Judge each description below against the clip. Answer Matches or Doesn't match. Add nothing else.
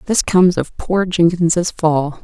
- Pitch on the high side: Doesn't match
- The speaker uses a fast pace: Doesn't match